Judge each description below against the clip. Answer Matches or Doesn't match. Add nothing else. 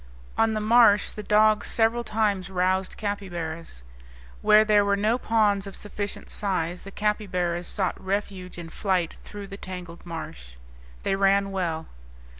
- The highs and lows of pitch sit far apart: Doesn't match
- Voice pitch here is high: Matches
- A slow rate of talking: Doesn't match